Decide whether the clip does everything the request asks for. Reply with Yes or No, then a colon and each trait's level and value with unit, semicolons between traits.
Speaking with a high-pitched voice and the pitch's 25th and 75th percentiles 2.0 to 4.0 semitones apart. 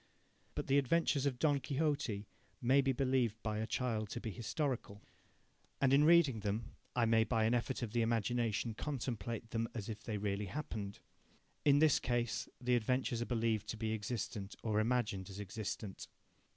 No: low, 115 Hz; average, 3.4 semitones